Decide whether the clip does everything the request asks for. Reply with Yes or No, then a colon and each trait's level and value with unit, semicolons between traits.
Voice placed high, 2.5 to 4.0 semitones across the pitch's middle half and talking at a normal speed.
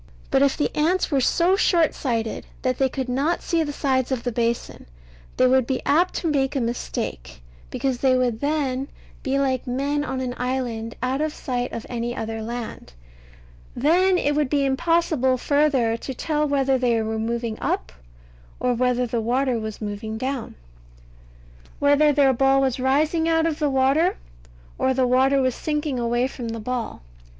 Yes: very high, 260 Hz; average, 3.2 semitones; average, 175 wpm